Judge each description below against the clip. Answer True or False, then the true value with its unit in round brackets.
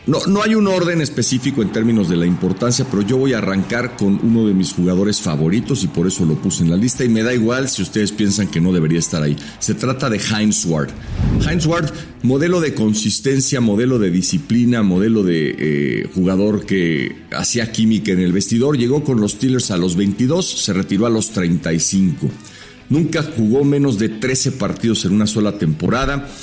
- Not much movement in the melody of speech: False (5.2 semitones)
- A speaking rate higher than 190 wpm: True (200 wpm)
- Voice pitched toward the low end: True (110 Hz)